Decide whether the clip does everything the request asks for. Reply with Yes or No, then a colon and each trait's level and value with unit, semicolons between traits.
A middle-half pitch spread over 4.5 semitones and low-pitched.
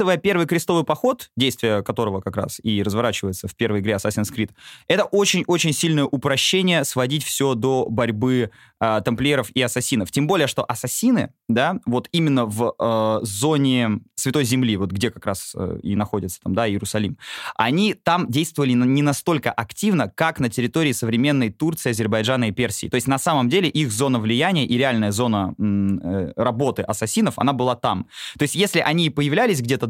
Yes: average, 5.0 semitones; low, 125 Hz